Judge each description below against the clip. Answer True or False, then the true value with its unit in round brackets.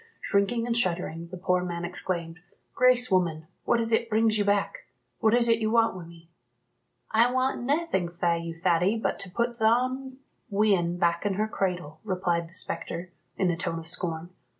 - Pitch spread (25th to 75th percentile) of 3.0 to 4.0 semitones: False (5.1 semitones)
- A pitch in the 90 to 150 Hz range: False (190 Hz)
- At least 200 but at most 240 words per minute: False (185 wpm)